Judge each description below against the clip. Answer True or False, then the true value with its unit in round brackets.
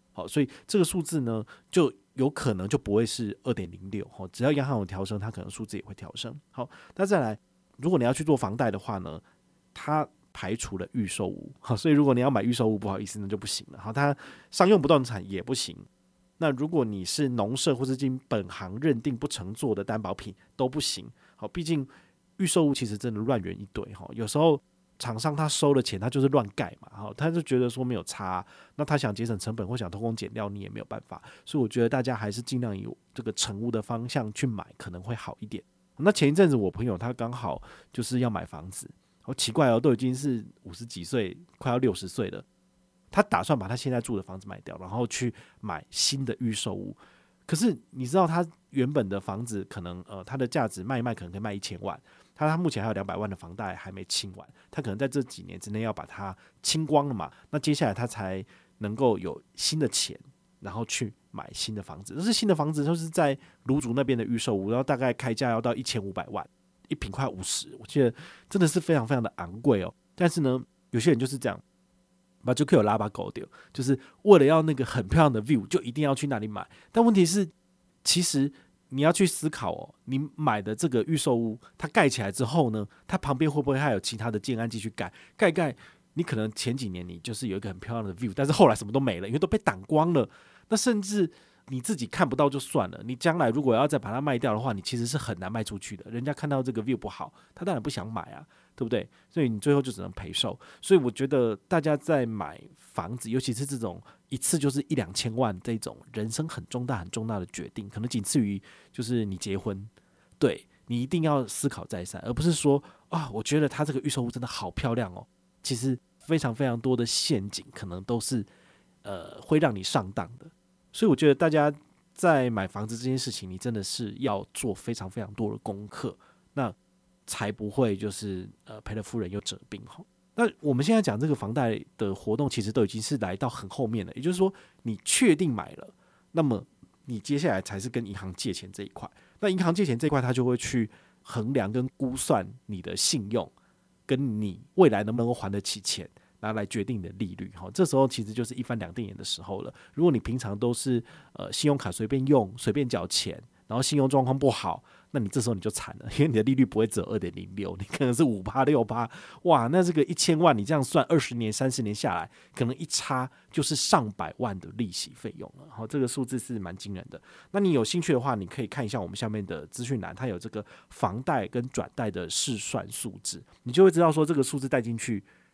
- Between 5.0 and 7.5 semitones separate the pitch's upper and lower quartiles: True (5.5 semitones)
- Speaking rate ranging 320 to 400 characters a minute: True (330 characters per minute)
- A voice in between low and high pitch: False (120 Hz)